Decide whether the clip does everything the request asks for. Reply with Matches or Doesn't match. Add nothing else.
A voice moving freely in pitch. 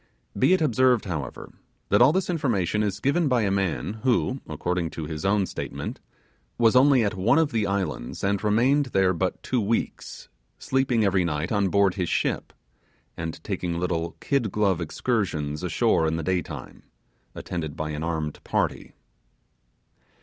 Matches